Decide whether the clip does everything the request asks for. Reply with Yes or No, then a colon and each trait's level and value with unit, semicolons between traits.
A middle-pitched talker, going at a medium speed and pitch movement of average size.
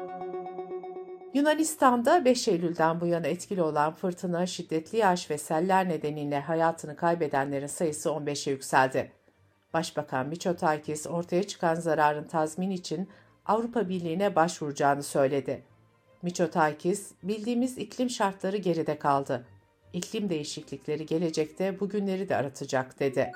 Yes: medium, 165 Hz; average, 110 wpm; average, 4.3 semitones